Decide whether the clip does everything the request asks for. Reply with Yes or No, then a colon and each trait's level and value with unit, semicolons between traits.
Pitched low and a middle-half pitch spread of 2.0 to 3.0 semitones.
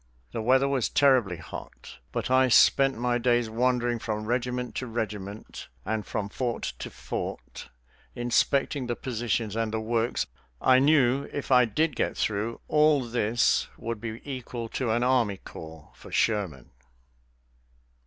Yes: low, 120 Hz; average, 2.7 semitones